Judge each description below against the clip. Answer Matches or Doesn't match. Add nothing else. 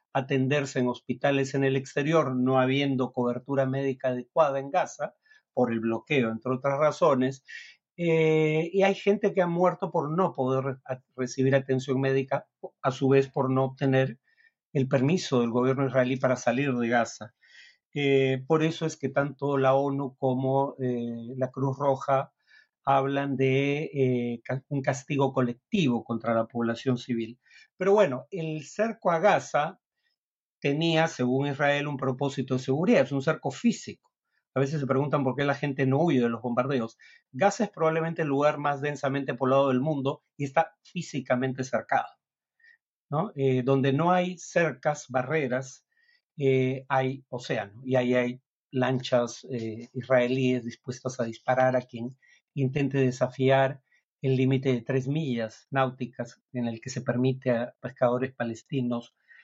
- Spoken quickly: Doesn't match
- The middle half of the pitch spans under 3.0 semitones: Matches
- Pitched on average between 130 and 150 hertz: Matches